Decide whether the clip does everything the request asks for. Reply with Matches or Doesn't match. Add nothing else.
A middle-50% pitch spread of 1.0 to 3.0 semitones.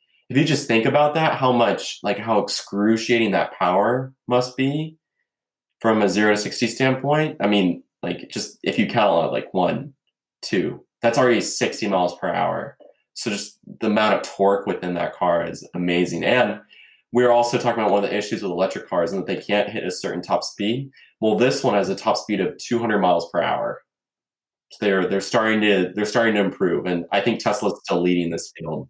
Doesn't match